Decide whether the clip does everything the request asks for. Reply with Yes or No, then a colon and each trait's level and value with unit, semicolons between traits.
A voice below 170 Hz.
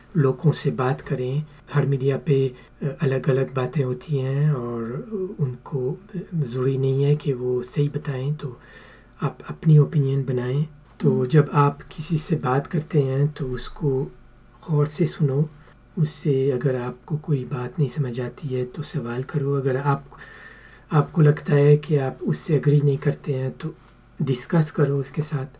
Yes: medium, 140 Hz